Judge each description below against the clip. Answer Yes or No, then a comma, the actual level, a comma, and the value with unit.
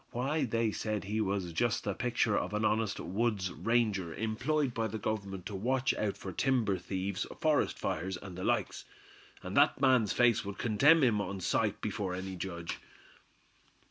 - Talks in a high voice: No, low, 105 Hz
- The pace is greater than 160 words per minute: Yes, average, 175 wpm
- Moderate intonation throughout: Yes, average, 3.7 semitones